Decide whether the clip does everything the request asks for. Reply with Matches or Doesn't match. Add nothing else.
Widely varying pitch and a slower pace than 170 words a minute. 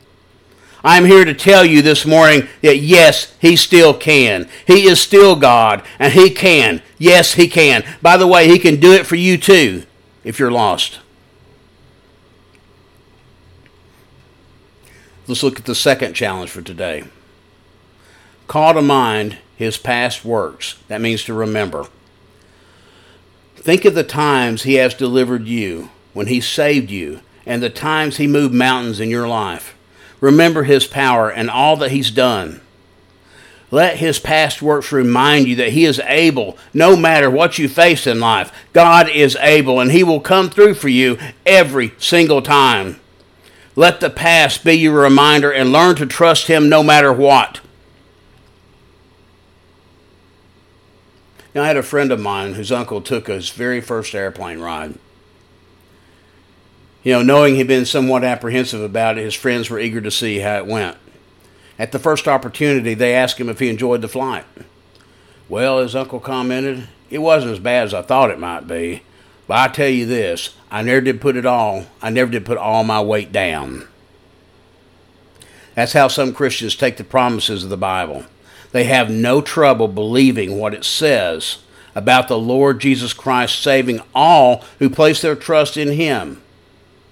Matches